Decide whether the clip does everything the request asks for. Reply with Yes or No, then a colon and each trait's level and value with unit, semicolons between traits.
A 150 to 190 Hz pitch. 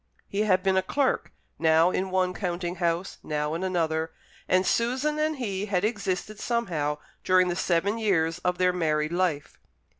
Yes: medium, 185 Hz